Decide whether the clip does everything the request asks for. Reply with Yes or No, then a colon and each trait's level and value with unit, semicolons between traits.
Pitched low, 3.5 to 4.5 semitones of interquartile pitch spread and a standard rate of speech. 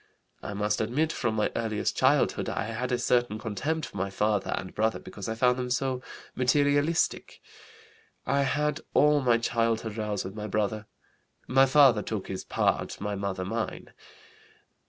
Yes: low, 115 Hz; average, 3.9 semitones; average, 160 wpm